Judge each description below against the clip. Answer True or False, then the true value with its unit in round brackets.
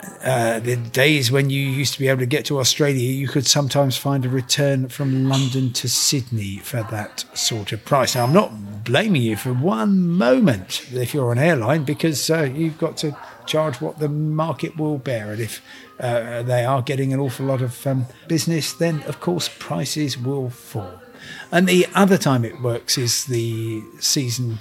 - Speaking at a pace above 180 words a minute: True (190 wpm)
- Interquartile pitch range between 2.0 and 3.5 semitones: False (4.0 semitones)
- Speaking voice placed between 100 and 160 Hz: True (135 Hz)